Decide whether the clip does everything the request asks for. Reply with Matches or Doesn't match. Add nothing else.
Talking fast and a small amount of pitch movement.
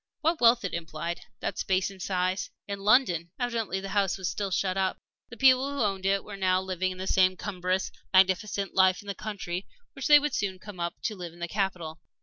Matches